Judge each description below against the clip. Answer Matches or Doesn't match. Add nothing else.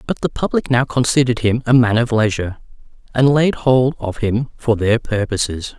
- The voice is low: Matches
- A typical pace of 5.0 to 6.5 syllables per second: Matches